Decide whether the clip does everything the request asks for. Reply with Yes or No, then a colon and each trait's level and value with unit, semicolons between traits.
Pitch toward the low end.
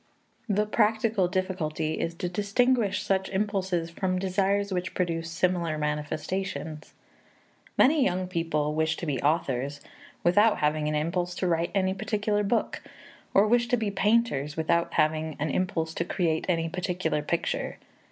No: medium, 180 Hz